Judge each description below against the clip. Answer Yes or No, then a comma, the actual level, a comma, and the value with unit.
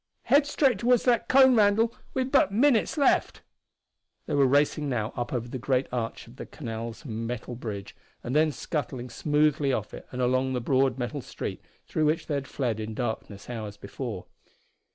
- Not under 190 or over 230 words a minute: No, average, 180 wpm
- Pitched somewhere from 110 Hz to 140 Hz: Yes, low, 135 Hz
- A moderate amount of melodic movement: No, wide, 5.7 semitones